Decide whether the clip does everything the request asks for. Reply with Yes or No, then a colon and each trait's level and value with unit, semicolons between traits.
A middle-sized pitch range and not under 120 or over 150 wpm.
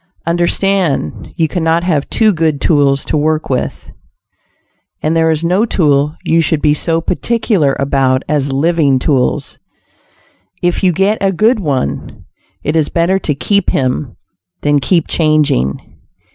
Yes: average, 3.6 semitones; average, 145 wpm